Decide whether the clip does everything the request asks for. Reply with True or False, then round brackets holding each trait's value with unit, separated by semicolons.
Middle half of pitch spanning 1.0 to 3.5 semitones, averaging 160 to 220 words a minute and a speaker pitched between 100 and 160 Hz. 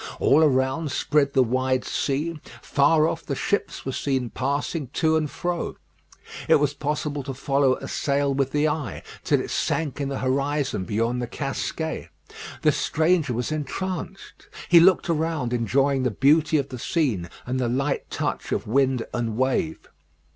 True (3.0 semitones; 165 wpm; 140 Hz)